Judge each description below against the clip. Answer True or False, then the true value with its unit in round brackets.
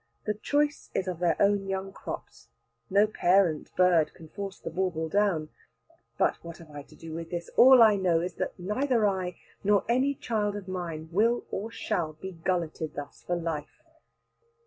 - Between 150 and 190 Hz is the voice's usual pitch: True (185 Hz)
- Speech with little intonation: False (3.8 semitones)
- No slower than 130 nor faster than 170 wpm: False (180 wpm)